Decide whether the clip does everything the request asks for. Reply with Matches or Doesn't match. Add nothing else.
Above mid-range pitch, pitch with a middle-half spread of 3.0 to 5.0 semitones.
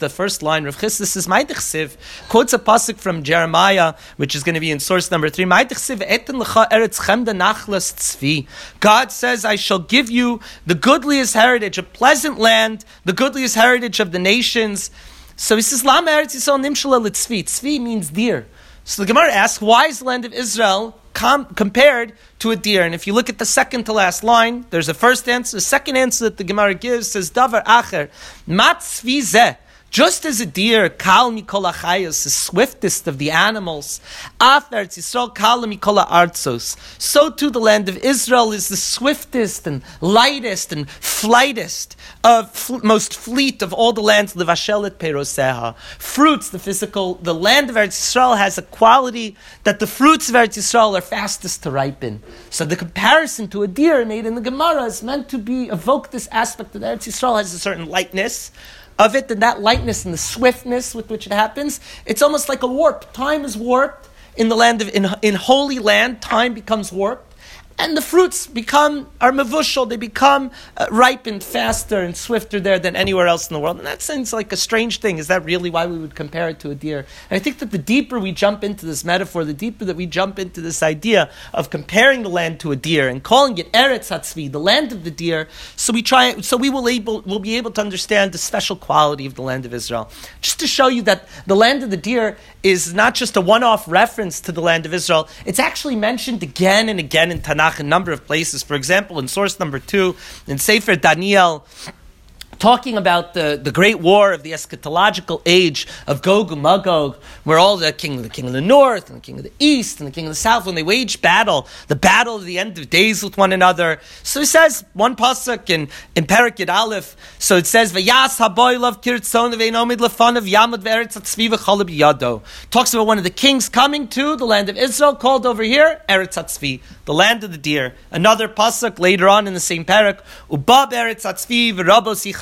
Doesn't match